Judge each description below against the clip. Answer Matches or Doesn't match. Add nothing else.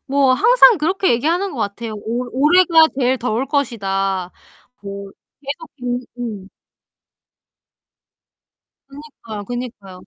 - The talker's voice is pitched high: Matches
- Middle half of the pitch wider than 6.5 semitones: Doesn't match